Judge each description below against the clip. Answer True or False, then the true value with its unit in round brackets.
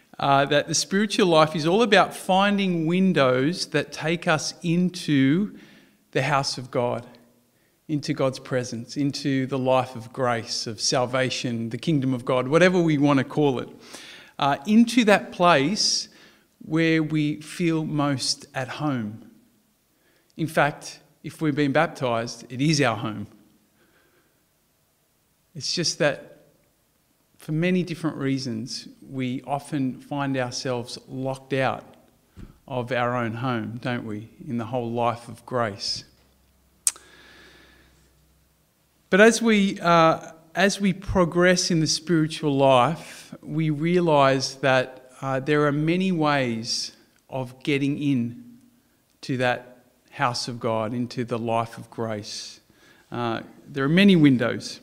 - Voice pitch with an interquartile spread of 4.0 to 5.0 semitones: True (4.7 semitones)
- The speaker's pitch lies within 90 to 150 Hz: True (140 Hz)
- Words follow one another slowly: True (130 wpm)